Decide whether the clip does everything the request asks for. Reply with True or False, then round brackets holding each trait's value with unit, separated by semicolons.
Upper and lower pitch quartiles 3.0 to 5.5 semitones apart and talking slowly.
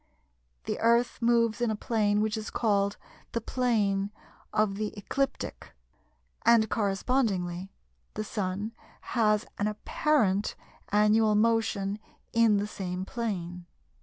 False (2.5 semitones; 115 wpm)